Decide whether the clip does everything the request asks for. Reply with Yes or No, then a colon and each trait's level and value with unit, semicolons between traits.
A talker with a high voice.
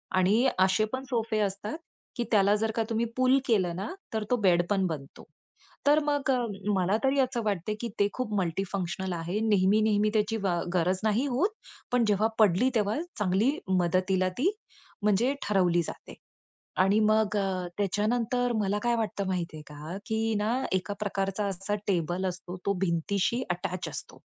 Yes: high, 205 Hz